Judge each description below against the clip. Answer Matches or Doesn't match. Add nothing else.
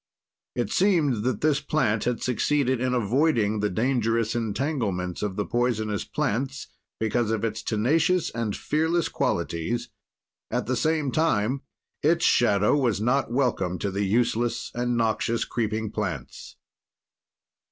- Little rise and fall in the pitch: Doesn't match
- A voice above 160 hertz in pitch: Doesn't match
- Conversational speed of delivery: Doesn't match